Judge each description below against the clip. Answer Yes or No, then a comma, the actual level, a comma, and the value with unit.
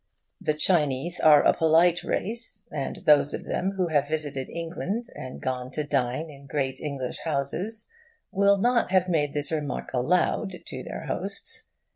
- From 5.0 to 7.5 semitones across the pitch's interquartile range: No, average, 4.4 semitones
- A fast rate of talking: No, average, 160 wpm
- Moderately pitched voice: Yes, medium, 155 Hz